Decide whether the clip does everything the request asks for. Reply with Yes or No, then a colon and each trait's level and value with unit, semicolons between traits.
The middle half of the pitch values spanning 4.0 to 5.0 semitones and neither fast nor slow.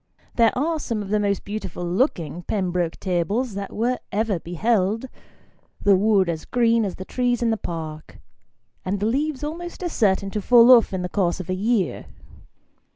Yes: average, 4.4 semitones; average, 180 wpm